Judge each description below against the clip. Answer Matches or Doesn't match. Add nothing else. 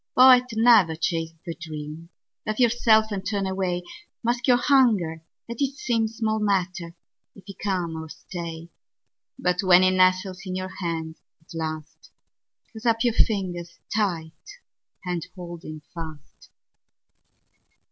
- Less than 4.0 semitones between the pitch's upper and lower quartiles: Doesn't match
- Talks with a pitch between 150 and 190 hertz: Matches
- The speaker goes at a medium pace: Doesn't match